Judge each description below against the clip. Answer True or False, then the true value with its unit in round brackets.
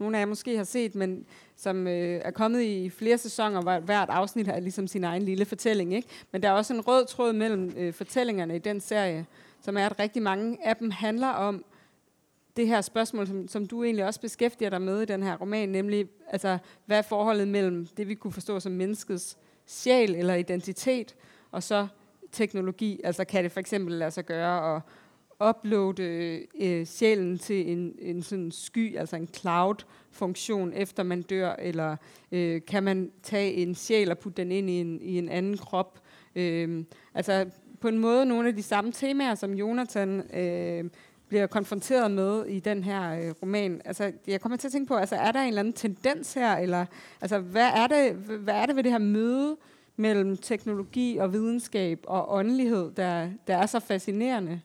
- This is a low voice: False (200 Hz)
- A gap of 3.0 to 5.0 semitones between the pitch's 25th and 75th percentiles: True (3.3 semitones)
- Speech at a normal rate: True (195 wpm)